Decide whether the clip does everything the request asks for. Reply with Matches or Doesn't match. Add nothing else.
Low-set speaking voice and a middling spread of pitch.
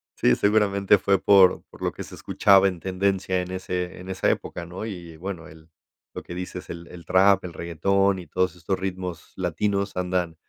Doesn't match